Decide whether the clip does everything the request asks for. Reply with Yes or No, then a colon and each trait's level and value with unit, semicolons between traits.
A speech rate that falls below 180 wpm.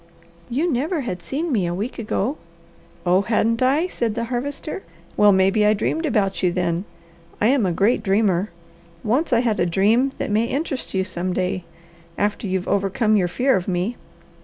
No: average, 185 wpm